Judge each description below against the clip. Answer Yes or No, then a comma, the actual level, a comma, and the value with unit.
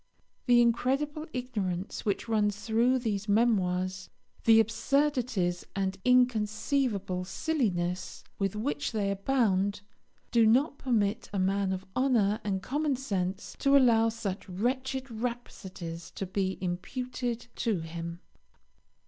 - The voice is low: No, high, 215 Hz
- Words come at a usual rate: No, slow, 115 wpm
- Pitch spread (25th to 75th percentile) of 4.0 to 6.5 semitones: Yes, average, 4.7 semitones